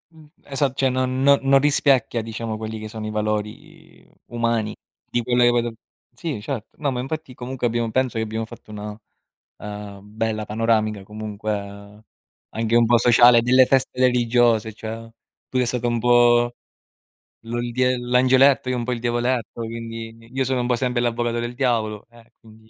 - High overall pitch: No, low, 120 Hz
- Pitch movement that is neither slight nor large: No, narrow, 2.2 semitones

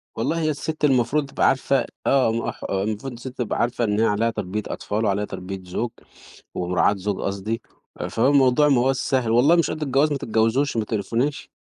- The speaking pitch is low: Yes, low, 115 Hz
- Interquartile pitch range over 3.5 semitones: Yes, average, 4.5 semitones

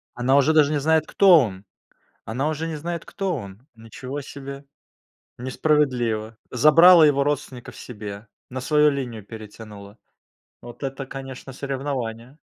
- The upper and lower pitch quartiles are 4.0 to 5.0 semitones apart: Yes, average, 4.6 semitones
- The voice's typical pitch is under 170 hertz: Yes, low, 135 Hz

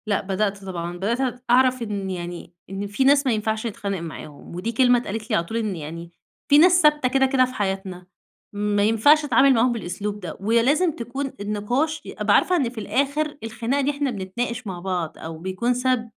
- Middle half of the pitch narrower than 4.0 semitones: No, average, 5.2 semitones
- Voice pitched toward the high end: Yes, high, 225 Hz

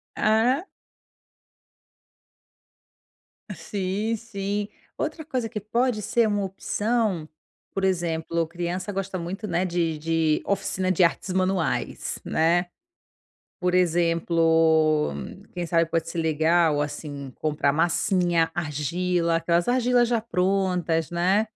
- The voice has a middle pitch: Yes, medium, 175 Hz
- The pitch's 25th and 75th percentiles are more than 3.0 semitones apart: Yes, average, 3.4 semitones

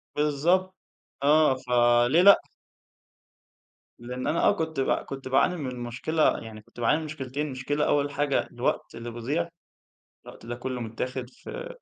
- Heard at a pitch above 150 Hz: No, low, 135 Hz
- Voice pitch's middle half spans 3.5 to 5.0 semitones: Yes, average, 3.9 semitones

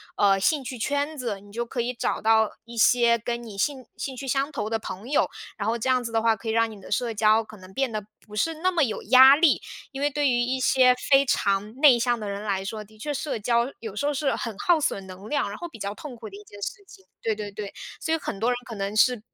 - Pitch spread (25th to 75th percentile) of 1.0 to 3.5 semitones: No, average, 4.0 semitones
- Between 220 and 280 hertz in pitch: Yes, high, 235 Hz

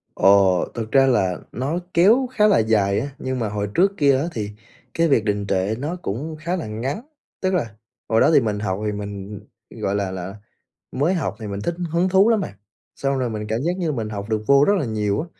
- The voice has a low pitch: Yes, low, 115 Hz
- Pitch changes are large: Yes, wide, 7.5 semitones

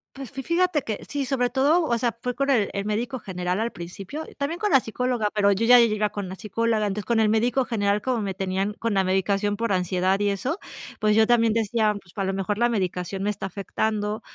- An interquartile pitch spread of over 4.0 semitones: No, average, 3.6 semitones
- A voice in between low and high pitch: No, high, 215 Hz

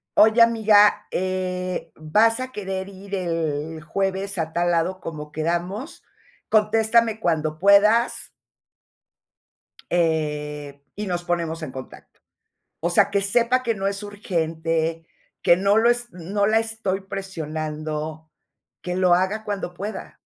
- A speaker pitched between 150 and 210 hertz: Yes, medium, 185 Hz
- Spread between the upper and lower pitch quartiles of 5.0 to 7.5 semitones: No, average, 4.3 semitones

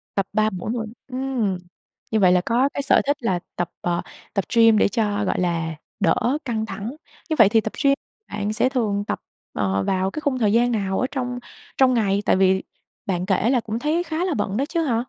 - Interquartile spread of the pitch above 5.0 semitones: No, average, 4.7 semitones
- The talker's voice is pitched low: No, high, 220 Hz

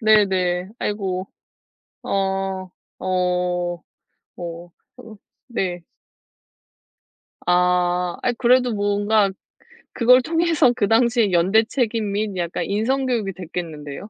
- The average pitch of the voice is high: Yes, high, 195 Hz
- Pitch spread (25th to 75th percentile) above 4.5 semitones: No, average, 3.9 semitones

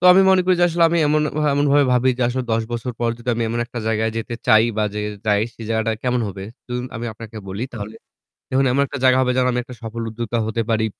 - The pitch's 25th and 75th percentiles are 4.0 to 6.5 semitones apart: No, narrow, 2.6 semitones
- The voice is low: Yes, low, 120 Hz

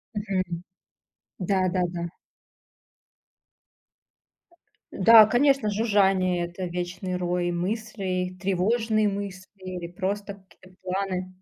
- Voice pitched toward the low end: No, high, 190 Hz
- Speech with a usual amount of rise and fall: No, narrow, 2.1 semitones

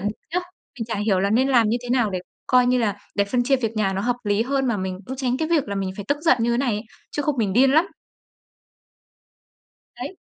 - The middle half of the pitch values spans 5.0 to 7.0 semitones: No, average, 4.3 semitones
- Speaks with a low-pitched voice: No, high, 235 Hz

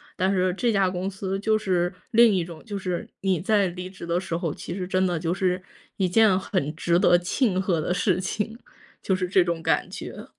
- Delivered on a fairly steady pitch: Yes, narrow, 1.9 semitones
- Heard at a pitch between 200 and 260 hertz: No, medium, 185 Hz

